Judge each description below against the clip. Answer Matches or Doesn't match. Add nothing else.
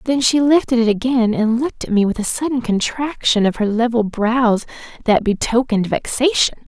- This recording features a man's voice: Doesn't match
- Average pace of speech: Matches